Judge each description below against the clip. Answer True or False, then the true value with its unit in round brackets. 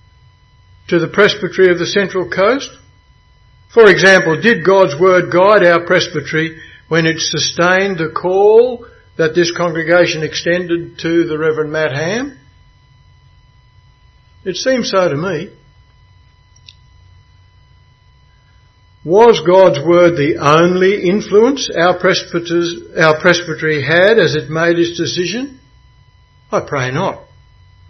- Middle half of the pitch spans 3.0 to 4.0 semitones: True (3.4 semitones)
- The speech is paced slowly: True (115 wpm)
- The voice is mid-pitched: True (170 Hz)